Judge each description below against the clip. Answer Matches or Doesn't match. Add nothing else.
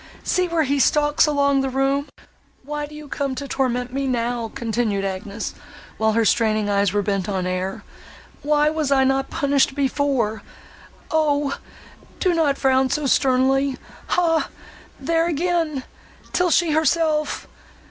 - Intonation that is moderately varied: Matches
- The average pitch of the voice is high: Matches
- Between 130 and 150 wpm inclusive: Matches